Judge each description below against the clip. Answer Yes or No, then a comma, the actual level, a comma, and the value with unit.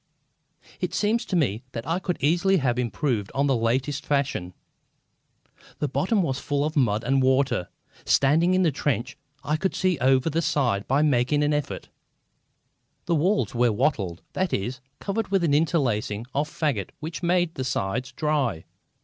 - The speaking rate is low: No, average, 165 wpm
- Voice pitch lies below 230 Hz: Yes, medium, 140 Hz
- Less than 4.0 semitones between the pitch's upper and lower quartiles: No, average, 5.0 semitones